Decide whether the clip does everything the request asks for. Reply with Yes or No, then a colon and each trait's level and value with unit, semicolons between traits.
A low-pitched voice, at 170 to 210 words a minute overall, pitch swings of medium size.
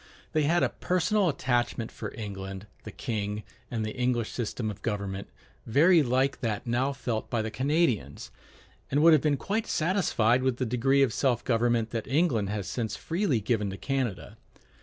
Yes: low, 120 Hz; average, 175 wpm; average, 4.5 semitones